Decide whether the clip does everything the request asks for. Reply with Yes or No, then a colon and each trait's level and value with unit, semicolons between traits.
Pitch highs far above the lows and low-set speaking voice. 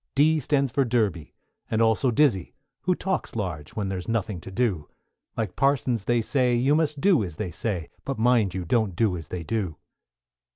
Yes: wide, 6.2 semitones; low, 115 Hz